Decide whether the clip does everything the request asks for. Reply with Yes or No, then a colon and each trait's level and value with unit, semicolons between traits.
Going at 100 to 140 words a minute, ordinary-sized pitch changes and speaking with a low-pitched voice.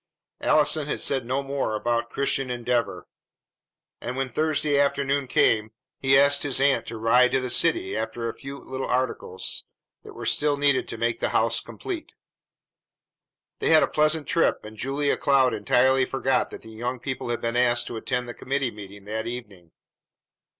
No: average, 175 wpm; average, 3.2 semitones; low, 125 Hz